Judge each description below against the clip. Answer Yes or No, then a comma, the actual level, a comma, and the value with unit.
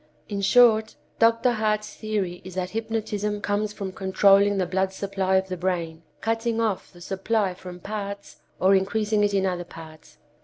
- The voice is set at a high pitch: Yes, high, 200 Hz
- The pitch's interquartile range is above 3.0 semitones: No, narrow, 2.4 semitones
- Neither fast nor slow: Yes, average, 165 wpm